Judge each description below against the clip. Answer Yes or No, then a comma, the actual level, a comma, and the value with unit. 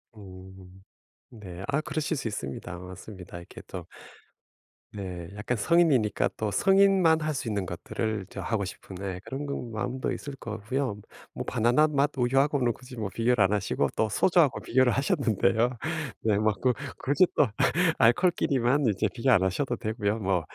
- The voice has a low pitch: Yes, low, 115 Hz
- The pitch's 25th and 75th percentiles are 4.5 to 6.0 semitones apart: Yes, wide, 5.6 semitones